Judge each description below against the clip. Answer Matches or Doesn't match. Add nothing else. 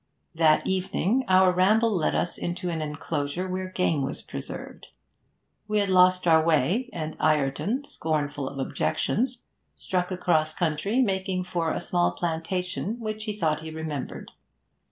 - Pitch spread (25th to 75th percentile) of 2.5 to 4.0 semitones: Matches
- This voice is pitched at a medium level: Matches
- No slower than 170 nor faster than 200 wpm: Doesn't match